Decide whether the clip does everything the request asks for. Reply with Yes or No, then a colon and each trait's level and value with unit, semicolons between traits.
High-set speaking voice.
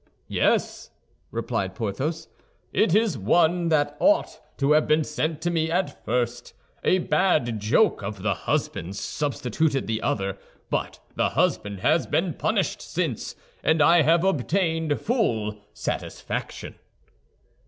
No: medium, 150 Hz